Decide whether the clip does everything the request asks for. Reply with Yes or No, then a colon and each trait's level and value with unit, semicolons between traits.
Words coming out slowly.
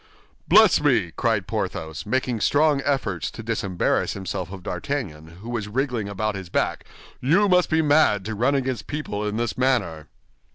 No: average, 165 wpm